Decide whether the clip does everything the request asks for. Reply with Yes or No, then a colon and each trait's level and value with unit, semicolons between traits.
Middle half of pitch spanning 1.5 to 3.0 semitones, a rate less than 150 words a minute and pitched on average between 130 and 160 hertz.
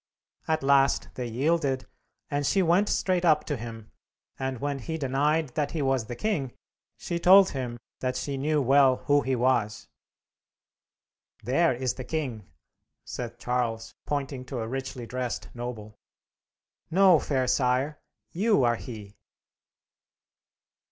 No: average, 3.7 semitones; average, 140 wpm; low, 135 Hz